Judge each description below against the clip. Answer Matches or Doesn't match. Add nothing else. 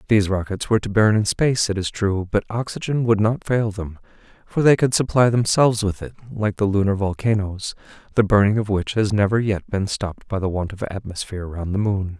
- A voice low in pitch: Matches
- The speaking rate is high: Matches